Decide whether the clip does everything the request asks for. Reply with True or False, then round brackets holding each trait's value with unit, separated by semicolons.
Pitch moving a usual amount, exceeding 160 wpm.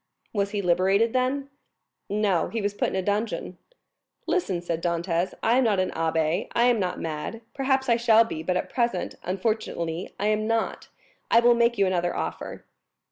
True (4.7 semitones; 185 wpm)